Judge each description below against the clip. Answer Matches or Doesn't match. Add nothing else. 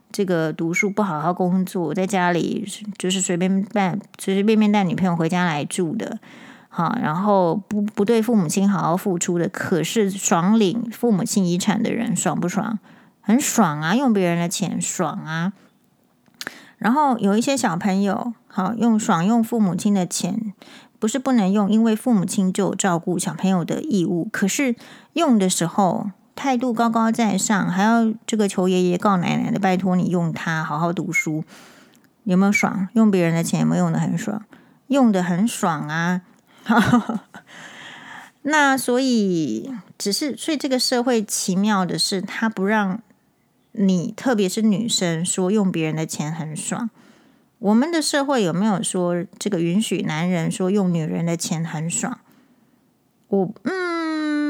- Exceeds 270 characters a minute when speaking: Doesn't match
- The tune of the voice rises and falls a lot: Doesn't match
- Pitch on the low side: Doesn't match